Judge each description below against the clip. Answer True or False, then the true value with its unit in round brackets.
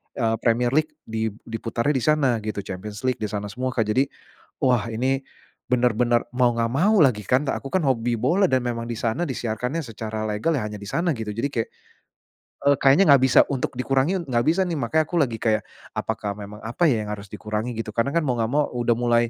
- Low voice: True (120 Hz)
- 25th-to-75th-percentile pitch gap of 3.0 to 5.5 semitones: True (3.7 semitones)